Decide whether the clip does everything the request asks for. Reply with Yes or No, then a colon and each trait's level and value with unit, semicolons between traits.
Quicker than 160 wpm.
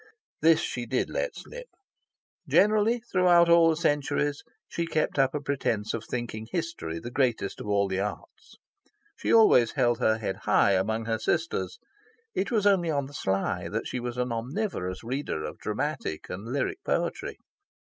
Yes: average, 170 wpm